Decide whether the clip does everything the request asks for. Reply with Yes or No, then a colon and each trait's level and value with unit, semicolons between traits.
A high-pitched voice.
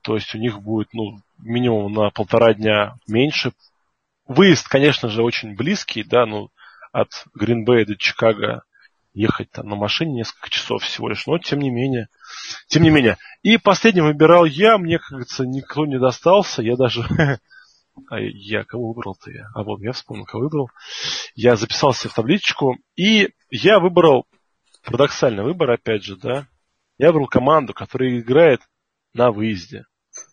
No: low, 125 Hz